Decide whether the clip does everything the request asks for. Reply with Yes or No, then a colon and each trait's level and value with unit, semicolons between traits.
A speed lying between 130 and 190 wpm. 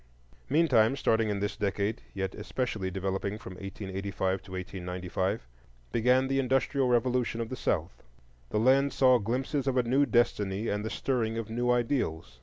Yes: average, 160 wpm